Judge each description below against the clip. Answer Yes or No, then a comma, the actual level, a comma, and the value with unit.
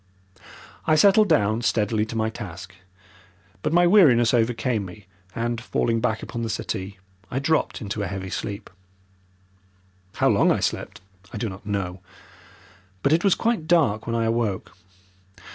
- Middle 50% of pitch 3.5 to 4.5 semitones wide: No, average, 4.9 semitones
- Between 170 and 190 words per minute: No, average, 155 wpm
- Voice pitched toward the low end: Yes, low, 115 Hz